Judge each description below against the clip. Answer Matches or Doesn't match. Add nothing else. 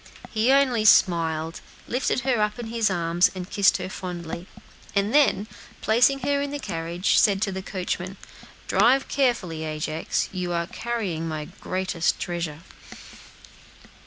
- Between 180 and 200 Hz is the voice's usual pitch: Matches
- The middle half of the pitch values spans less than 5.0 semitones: Doesn't match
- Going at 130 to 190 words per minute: Matches